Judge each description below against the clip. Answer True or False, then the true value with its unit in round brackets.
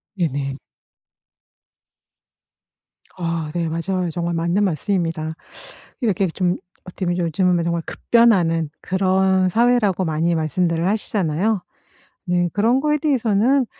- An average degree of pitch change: True (3.5 semitones)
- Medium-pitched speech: True (180 Hz)